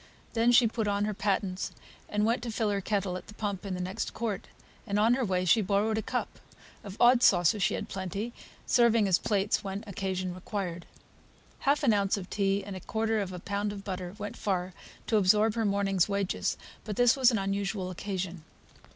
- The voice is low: No, high, 200 Hz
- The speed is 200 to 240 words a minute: Yes, fast, 205 wpm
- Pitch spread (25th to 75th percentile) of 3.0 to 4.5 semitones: No, narrow, 2.6 semitones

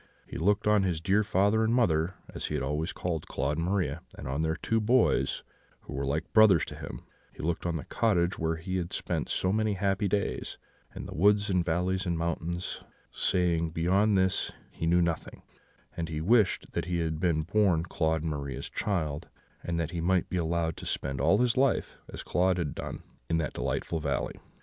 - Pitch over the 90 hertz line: No, very low, 85 Hz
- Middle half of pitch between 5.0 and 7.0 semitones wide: No, average, 3.4 semitones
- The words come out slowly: No, average, 200 wpm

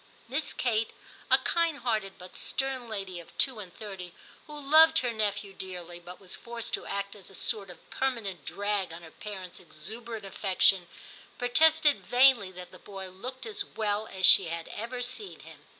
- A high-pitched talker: Yes, high, 210 Hz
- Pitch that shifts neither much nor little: Yes, average, 4.8 semitones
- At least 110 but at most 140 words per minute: No, average, 180 wpm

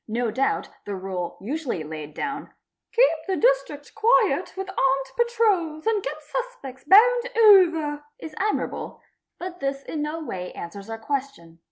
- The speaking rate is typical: Yes, average, 160 wpm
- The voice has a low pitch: No, very high, 300 Hz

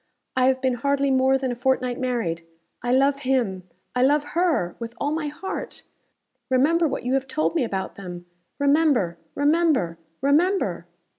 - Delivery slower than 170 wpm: Yes, average, 160 wpm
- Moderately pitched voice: No, very high, 265 Hz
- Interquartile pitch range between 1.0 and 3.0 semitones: No, average, 3.5 semitones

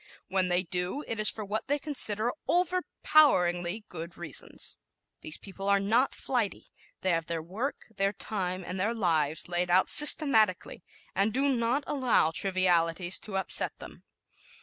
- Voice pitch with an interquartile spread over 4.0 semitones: Yes, average, 4.8 semitones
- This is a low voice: No, high, 195 Hz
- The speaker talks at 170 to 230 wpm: No, average, 150 wpm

